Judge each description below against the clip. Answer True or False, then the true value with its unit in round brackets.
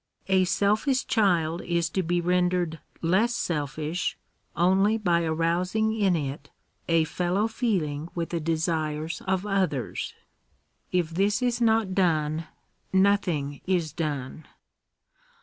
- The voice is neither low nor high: True (175 Hz)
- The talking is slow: True (115 wpm)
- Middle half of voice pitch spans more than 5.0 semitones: False (3.6 semitones)